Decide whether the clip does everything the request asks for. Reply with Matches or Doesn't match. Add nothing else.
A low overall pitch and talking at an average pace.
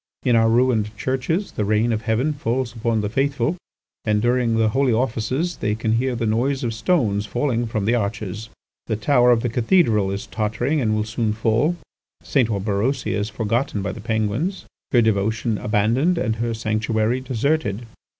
Matches